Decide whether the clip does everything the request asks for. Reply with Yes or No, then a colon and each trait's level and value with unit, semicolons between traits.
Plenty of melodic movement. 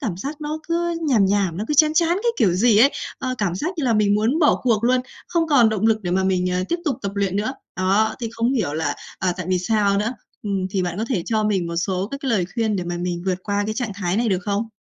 No: average, 4.8 semitones